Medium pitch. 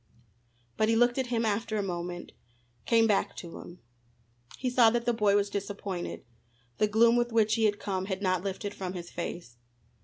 No: high, 205 Hz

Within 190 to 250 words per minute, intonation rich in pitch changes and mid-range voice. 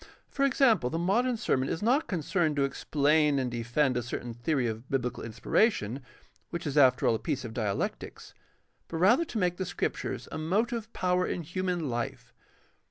No: average, 175 wpm; wide, 6.9 semitones; medium, 155 Hz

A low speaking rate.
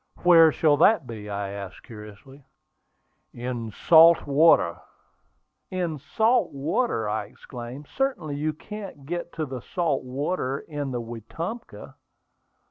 Yes: slow, 130 wpm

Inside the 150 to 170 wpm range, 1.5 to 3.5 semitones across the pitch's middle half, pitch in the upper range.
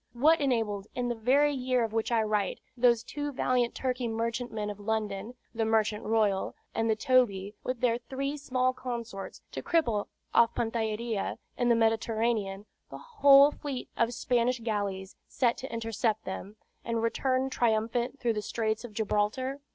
Yes: average, 160 wpm; average, 2.7 semitones; high, 230 Hz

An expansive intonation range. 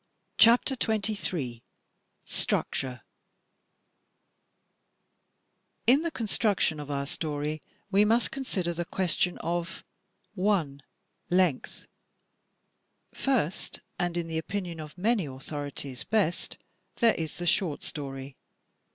Yes: wide, 6.0 semitones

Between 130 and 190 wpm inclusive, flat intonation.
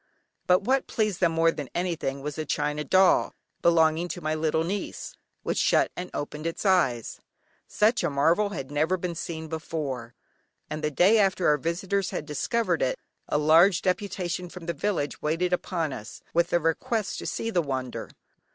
No: average, 180 wpm; average, 3.6 semitones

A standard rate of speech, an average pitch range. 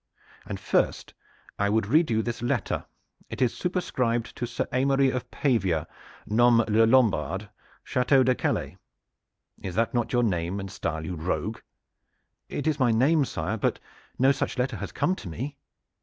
Yes: average, 165 wpm; average, 4.4 semitones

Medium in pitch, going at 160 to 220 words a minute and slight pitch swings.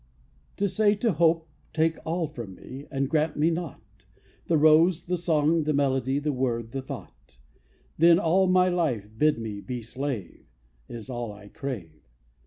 No: medium, 150 Hz; average, 165 wpm; wide, 5.4 semitones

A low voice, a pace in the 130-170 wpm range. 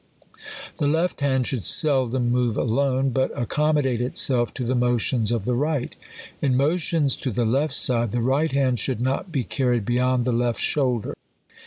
No: low, 130 Hz; average, 185 wpm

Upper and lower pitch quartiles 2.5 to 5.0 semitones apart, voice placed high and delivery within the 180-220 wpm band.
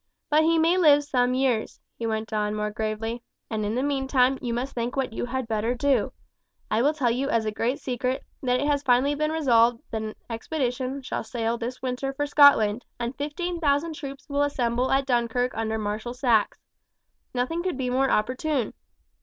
Yes: average, 3.6 semitones; very high, 250 Hz; average, 195 wpm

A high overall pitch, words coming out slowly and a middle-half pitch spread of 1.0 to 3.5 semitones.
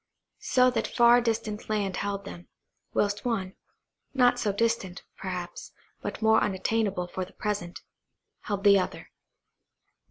Yes: high, 205 Hz; slow, 120 wpm; average, 3.1 semitones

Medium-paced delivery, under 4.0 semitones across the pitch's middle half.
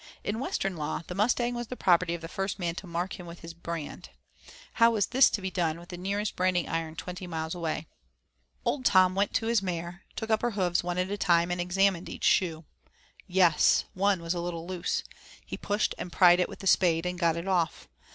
No: fast, 225 wpm; narrow, 2.4 semitones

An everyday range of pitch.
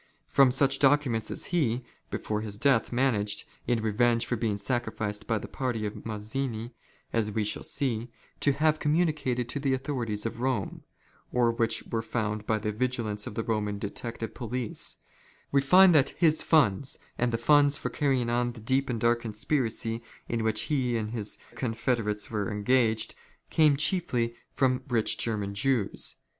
Yes: average, 3.5 semitones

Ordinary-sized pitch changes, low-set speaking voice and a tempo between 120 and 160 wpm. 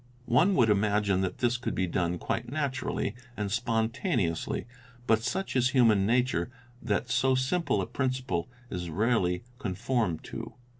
Yes: average, 4.8 semitones; low, 115 Hz; average, 150 wpm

